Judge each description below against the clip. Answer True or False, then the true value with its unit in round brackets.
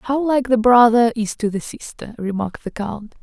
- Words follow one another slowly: False (205 wpm)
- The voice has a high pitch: True (230 Hz)